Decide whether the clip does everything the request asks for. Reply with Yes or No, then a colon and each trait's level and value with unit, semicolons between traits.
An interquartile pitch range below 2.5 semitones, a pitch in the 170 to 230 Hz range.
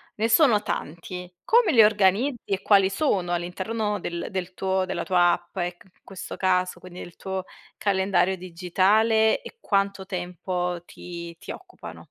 No: average, 2.8 semitones; high, 190 Hz